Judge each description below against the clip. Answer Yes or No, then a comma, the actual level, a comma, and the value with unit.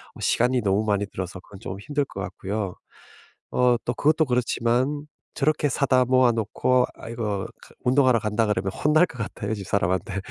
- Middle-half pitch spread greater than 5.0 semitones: No, average, 4.2 semitones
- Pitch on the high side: No, low, 115 Hz